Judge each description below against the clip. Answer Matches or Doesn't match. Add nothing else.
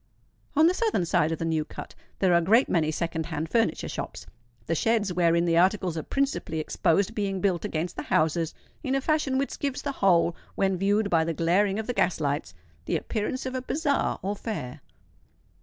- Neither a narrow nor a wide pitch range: Doesn't match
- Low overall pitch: Doesn't match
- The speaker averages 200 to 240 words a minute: Matches